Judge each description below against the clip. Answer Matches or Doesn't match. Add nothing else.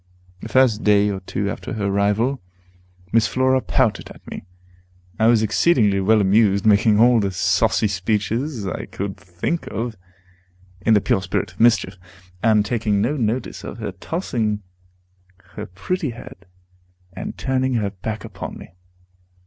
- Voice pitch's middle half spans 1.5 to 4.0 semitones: Matches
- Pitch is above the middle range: Doesn't match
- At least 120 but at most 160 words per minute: Matches